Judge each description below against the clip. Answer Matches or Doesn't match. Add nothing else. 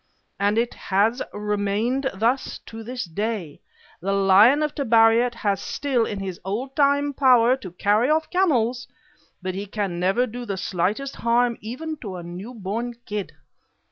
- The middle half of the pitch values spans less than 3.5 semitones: Doesn't match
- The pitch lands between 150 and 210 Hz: Doesn't match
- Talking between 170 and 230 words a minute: Doesn't match